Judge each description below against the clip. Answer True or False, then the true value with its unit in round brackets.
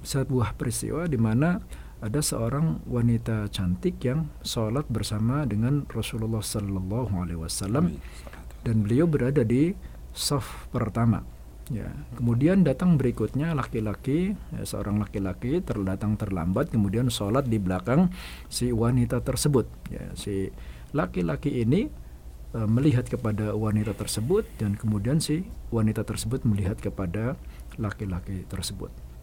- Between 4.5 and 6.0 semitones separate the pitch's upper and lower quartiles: True (5.0 semitones)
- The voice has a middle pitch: False (110 Hz)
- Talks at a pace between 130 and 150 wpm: False (115 wpm)